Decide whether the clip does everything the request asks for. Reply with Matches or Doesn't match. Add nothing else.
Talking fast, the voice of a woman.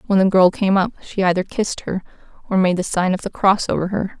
Matches